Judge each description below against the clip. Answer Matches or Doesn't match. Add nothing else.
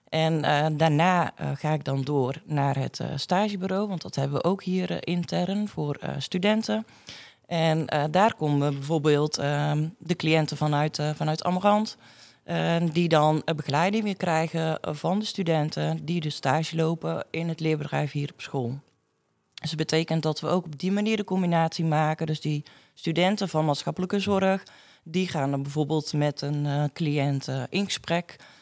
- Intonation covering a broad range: Doesn't match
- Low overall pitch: Doesn't match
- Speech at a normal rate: Matches